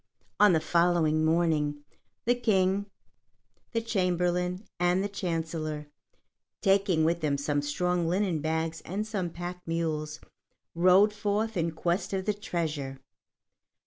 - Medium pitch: Yes, medium, 175 Hz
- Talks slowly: Yes, slow, 125 wpm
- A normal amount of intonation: Yes, average, 3.3 semitones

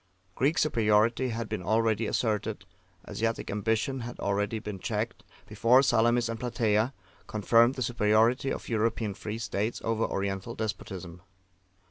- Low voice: Yes, low, 110 Hz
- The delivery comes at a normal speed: No, slow, 130 wpm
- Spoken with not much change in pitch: Yes, narrow, 2.0 semitones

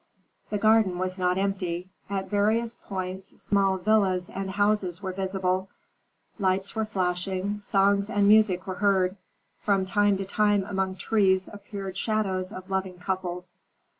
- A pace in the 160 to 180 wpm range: No, average, 140 wpm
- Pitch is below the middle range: No, high, 195 Hz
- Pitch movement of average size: No, narrow, 1.6 semitones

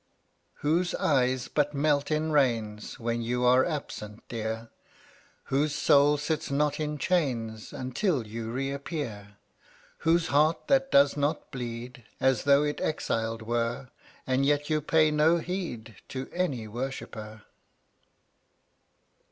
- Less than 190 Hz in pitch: Yes, medium, 140 Hz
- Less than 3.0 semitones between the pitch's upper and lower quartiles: No, average, 4.5 semitones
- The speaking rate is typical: No, slow, 125 wpm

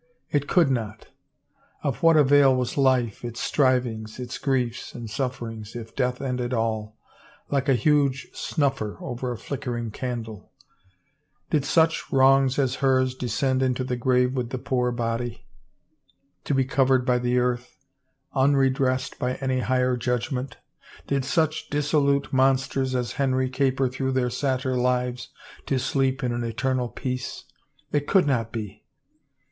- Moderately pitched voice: No, low, 130 Hz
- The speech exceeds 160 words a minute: No, average, 150 wpm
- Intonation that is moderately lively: No, narrow, 1.8 semitones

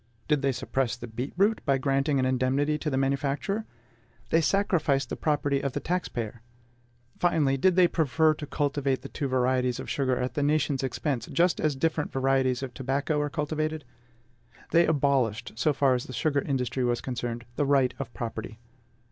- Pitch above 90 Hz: Yes, medium, 140 Hz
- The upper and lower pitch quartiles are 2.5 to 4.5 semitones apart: Yes, average, 2.9 semitones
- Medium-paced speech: Yes, average, 180 wpm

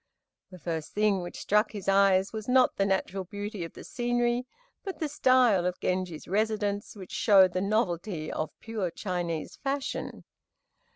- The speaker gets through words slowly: No, average, 160 wpm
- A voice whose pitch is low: No, high, 200 Hz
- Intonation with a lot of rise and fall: No, average, 3.6 semitones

